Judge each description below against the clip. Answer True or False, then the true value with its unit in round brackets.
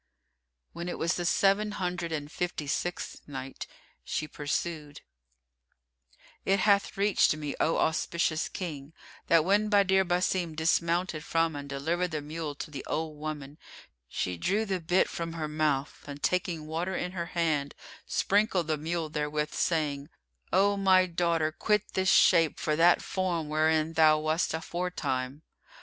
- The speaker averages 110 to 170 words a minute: True (150 wpm)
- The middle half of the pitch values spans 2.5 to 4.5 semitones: True (2.9 semitones)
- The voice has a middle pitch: True (165 Hz)